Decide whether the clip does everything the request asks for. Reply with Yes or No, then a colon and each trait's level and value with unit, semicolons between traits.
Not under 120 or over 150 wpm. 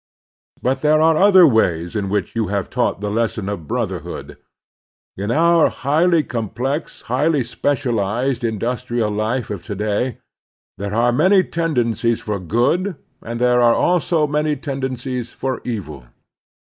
Yes: average, 140 wpm